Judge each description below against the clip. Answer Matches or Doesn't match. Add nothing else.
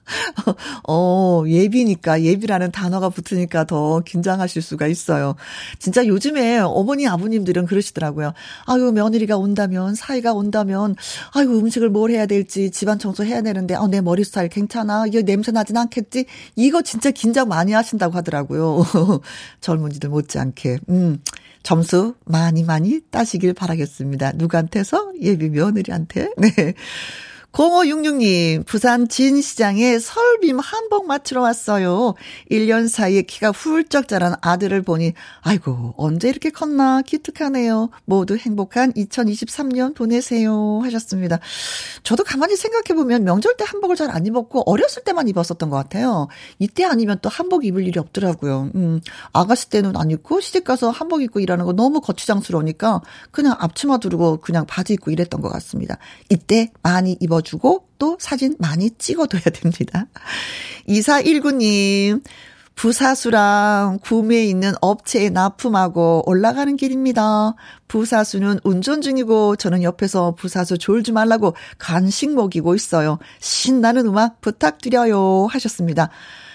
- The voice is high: Matches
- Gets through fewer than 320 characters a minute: Doesn't match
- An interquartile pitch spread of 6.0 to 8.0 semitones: Doesn't match